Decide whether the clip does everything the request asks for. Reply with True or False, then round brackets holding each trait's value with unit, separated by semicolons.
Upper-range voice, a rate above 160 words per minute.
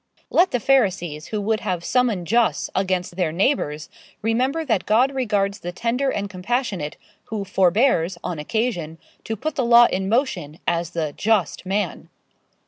False (200 Hz; 155 wpm)